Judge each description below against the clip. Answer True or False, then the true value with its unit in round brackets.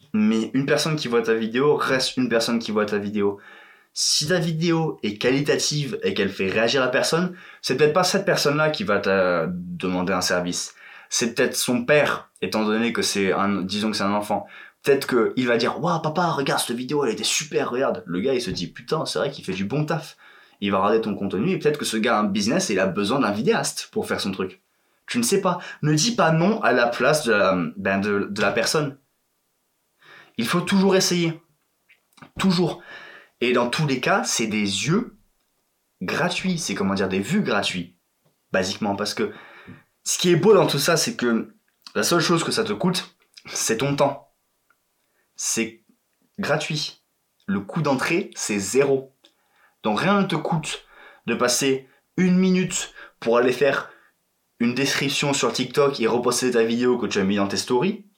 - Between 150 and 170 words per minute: False (200 wpm)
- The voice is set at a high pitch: False (140 Hz)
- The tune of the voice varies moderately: False (7.9 semitones)